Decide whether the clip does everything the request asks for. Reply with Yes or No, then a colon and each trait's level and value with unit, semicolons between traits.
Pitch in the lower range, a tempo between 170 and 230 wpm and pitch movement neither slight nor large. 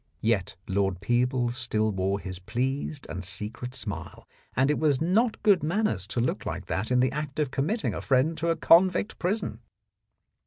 No: low, 130 Hz; average, 180 wpm; wide, 6.7 semitones